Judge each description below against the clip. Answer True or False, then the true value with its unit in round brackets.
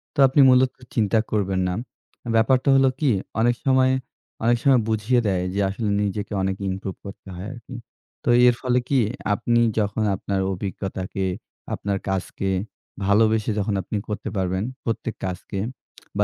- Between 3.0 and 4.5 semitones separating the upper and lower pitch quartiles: True (3.9 semitones)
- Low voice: True (105 Hz)